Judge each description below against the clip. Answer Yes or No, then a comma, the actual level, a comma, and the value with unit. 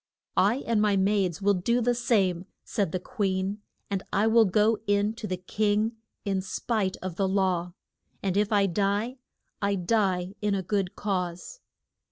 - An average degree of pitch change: No, narrow, 2.3 semitones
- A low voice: No, high, 200 Hz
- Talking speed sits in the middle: Yes, average, 170 wpm